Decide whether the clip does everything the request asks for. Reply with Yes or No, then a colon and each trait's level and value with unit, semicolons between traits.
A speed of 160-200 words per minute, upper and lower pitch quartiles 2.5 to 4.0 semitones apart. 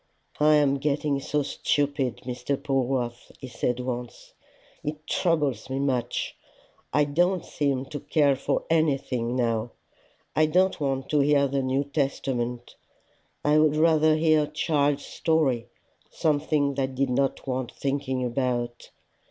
No: slow, 135 wpm; average, 2.8 semitones